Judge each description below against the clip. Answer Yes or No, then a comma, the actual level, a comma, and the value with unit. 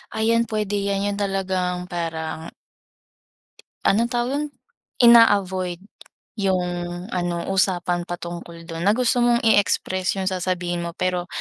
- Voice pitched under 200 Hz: Yes, medium, 185 Hz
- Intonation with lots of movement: No, average, 2.9 semitones